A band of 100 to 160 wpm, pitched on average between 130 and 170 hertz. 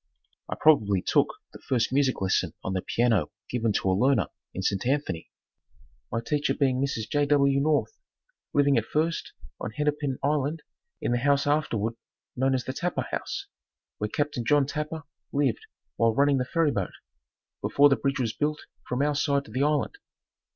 No: average, 175 wpm; medium, 140 Hz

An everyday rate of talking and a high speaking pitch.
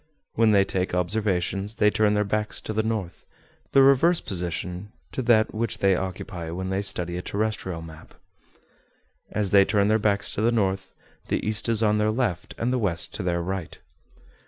No: average, 185 wpm; low, 100 Hz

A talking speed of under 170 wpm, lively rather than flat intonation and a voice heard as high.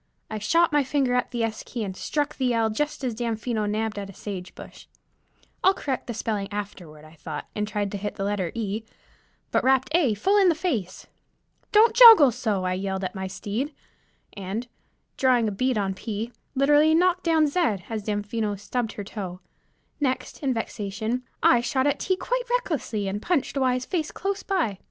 No: average, 190 wpm; wide, 6.0 semitones; high, 230 Hz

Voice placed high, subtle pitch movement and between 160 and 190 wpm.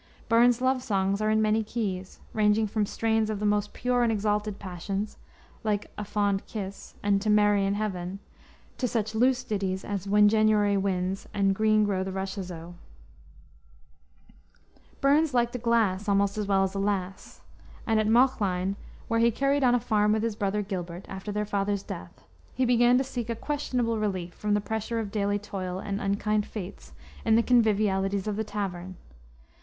Yes: high, 210 Hz; narrow, 2.2 semitones; average, 180 wpm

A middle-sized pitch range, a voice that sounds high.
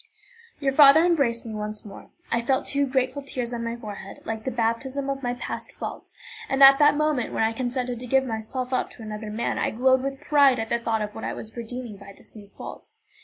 Yes: average, 3.4 semitones; high, 245 Hz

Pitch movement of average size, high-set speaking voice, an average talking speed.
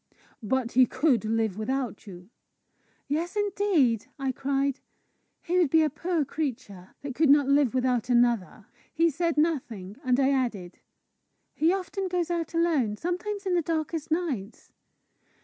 No: wide, 5.7 semitones; very high, 280 Hz; average, 150 wpm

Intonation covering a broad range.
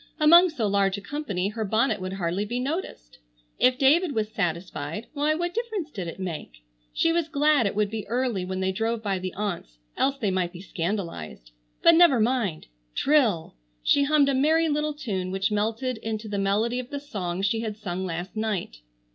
Yes: wide, 6.9 semitones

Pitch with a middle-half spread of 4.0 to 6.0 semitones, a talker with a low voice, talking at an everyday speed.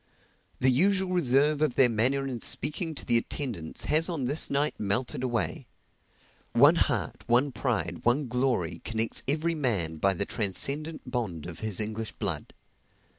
Yes: average, 5.2 semitones; low, 125 Hz; average, 155 wpm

